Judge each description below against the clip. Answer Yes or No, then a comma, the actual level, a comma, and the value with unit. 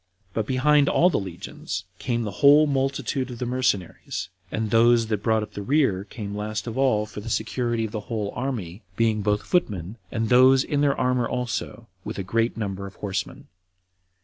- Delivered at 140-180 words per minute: No, average, 190 wpm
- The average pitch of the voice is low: Yes, low, 115 Hz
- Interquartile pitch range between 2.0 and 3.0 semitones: No, average, 3.6 semitones